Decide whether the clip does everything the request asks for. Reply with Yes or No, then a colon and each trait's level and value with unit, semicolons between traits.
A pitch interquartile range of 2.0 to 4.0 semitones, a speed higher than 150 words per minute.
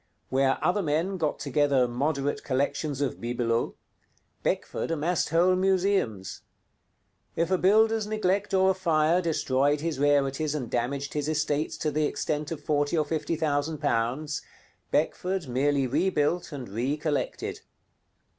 No: average, 3.4 semitones; slow, 135 wpm